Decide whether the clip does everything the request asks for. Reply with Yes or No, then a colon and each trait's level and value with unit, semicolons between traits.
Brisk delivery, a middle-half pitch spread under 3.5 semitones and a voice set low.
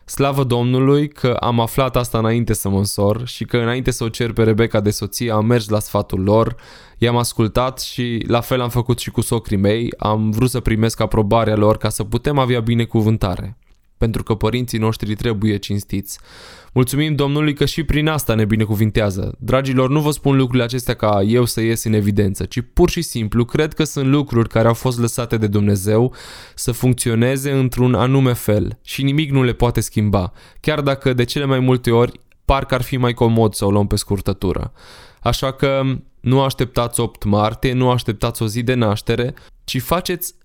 Yes: fast, 190 wpm; average, 2.9 semitones; low, 120 Hz